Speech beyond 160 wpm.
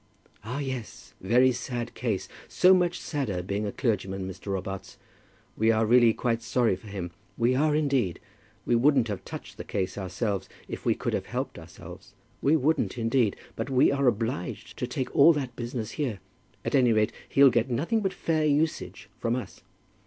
Yes: average, 180 wpm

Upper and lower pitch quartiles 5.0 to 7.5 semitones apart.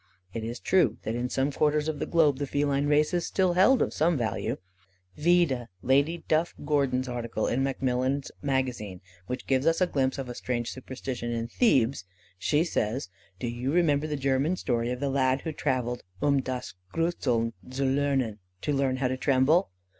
No: average, 3.2 semitones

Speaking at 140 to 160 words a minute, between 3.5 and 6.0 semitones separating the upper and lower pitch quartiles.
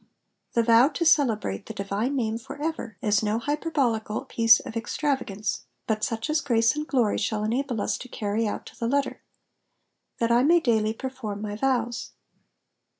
No: average, 175 wpm; average, 3.8 semitones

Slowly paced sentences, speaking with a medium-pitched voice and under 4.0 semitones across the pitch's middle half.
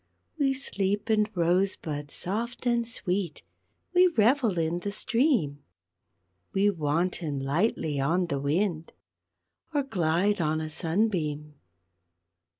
No: slow, 120 wpm; medium, 180 Hz; wide, 5.6 semitones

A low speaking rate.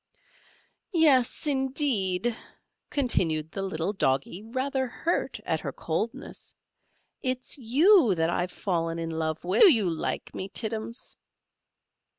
Yes: slow, 120 wpm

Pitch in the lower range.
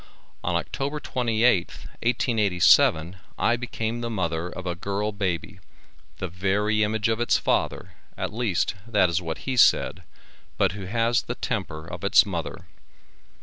Yes: low, 105 Hz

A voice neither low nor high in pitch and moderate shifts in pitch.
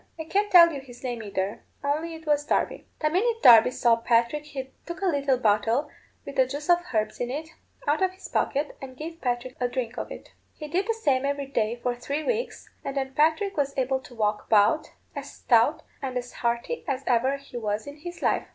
No: very high, 275 Hz; average, 4.2 semitones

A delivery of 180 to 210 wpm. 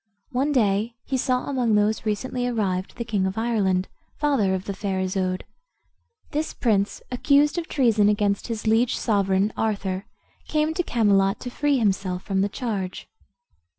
No: average, 155 wpm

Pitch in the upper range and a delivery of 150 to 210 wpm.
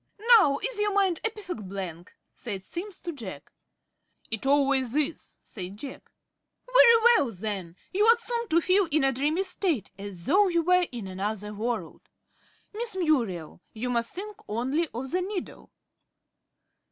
Yes: very high, 285 Hz; average, 155 wpm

